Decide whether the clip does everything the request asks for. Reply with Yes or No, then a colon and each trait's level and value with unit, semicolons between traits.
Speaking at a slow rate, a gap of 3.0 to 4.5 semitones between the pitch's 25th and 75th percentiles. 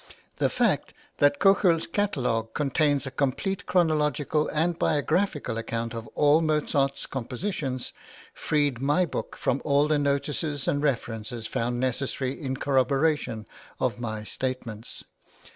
Yes: slow, 130 wpm; average, 3.6 semitones